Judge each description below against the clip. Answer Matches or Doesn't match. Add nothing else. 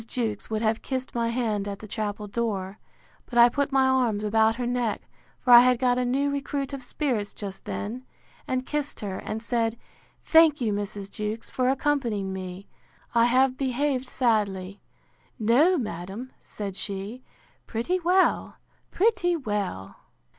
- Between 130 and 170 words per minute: Matches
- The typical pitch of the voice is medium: Doesn't match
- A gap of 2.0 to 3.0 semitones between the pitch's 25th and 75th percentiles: Doesn't match